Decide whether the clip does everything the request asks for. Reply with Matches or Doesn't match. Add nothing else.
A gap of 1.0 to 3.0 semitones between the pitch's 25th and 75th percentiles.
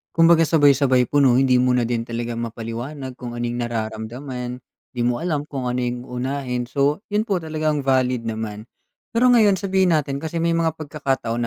Doesn't match